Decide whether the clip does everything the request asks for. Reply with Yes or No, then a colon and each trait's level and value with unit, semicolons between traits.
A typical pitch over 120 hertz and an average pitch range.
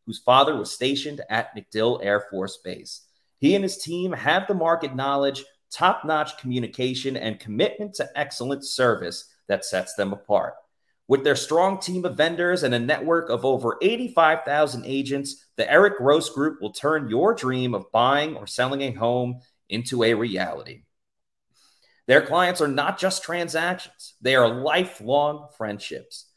Yes: medium, 140 Hz; average, 4.7 semitones